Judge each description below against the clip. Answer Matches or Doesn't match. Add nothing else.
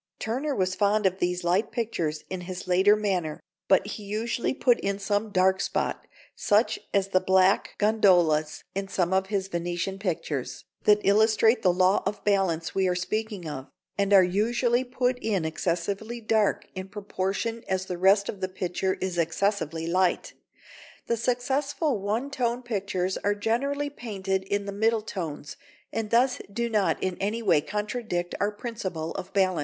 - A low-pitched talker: Doesn't match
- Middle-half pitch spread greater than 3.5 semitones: Doesn't match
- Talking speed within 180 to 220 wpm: Doesn't match